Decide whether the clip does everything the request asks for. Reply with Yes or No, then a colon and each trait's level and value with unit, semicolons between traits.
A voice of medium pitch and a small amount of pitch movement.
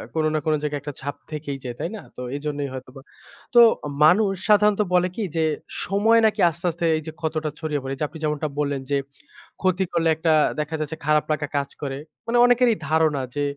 No: medium, 155 Hz; average, 3.7 semitones